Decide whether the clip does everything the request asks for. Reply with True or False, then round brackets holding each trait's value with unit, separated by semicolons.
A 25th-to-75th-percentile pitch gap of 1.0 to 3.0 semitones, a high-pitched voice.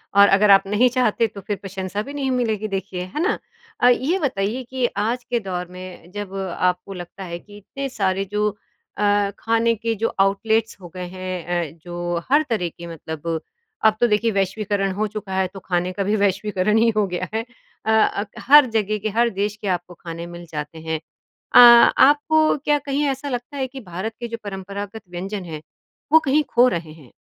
False (4.0 semitones; 205 Hz)